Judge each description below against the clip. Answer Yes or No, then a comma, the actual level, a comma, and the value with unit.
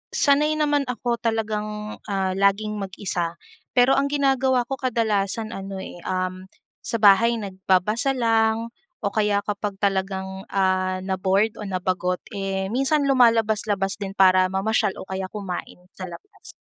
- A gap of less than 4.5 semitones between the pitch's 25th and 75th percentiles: Yes, average, 3.4 semitones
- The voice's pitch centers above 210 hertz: No, high, 205 Hz